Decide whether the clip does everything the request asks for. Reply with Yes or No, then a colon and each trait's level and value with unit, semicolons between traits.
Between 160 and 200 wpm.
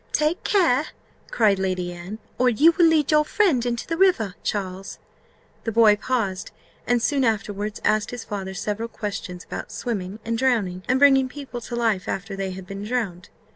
Yes: average, 175 wpm